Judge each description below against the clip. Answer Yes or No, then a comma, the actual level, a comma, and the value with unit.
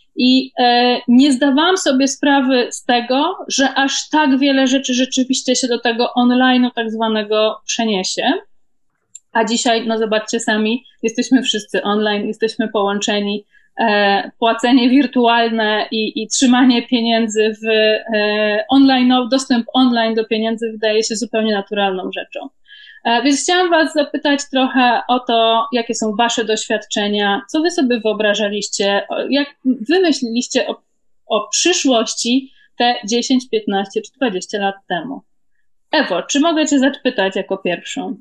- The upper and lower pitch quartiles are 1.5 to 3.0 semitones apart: No, average, 3.6 semitones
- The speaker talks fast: No, average, 130 wpm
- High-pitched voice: Yes, high, 240 Hz